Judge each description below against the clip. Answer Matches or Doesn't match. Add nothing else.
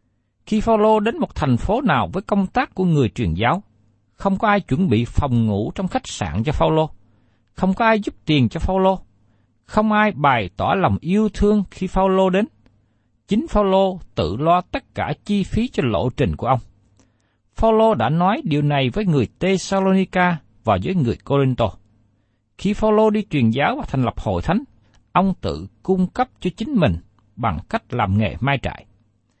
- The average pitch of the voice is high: Doesn't match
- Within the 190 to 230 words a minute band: Matches